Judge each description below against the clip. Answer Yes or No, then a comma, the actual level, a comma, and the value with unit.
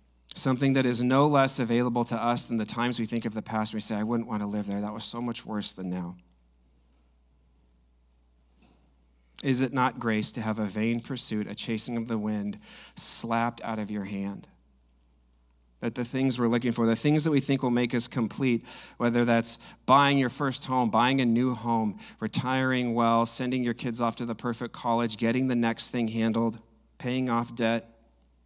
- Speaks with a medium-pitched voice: No, low, 115 Hz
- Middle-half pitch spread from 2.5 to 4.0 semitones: Yes, average, 2.8 semitones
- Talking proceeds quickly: No, average, 195 wpm